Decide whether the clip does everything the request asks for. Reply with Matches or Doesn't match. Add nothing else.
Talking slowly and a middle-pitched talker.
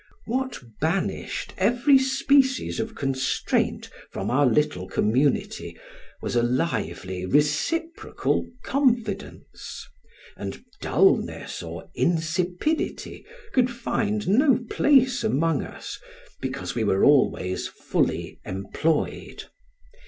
Matches